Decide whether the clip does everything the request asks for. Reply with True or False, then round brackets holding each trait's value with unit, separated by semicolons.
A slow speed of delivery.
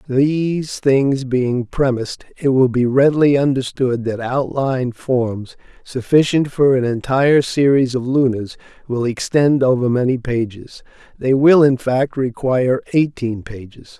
True (130 wpm)